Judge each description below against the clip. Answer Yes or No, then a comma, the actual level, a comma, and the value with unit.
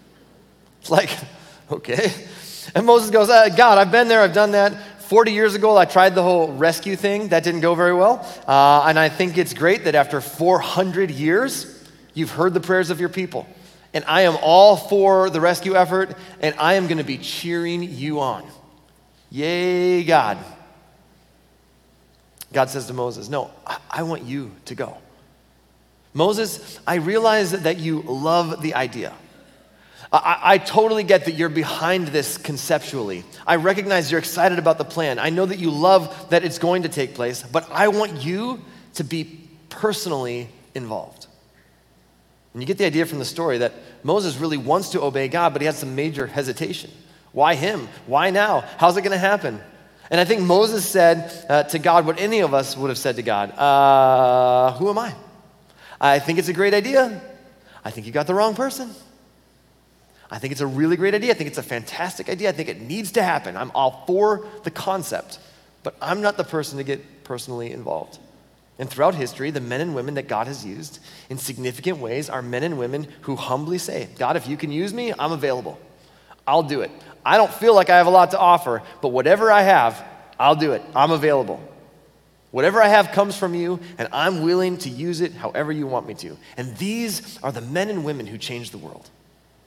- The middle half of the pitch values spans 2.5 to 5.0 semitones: No, wide, 5.4 semitones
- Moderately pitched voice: Yes, medium, 170 Hz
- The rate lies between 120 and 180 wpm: No, average, 195 wpm